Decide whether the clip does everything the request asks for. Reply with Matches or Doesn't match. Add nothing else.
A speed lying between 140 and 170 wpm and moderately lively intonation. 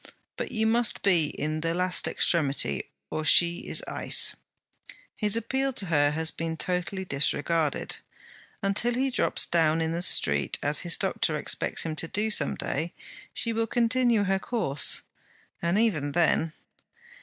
Doesn't match